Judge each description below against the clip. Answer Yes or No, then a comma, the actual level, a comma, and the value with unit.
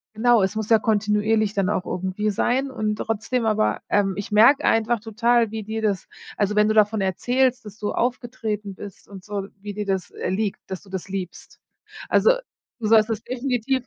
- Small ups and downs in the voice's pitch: Yes, narrow, 2.3 semitones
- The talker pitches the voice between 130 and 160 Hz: No, high, 215 Hz